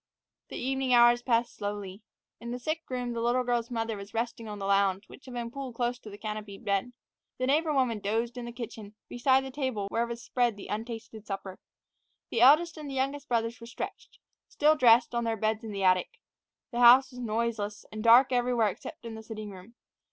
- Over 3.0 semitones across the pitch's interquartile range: No, average, 2.7 semitones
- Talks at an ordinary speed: No, fast, 210 wpm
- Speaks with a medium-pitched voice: No, high, 235 Hz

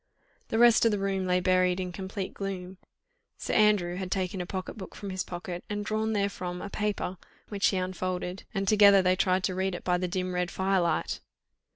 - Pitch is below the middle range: No, high, 190 Hz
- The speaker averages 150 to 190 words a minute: No, fast, 205 wpm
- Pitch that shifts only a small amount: Yes, narrow, 1.7 semitones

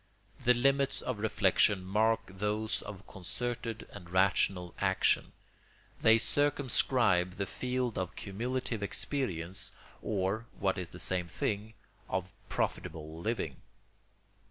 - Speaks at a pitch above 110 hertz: No, low, 100 Hz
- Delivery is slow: Yes, slow, 110 wpm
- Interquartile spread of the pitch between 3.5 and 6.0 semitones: Yes, average, 4.0 semitones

